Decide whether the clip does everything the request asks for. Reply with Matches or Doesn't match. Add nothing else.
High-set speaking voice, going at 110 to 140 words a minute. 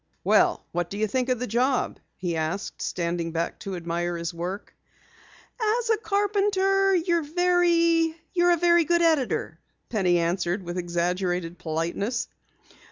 Matches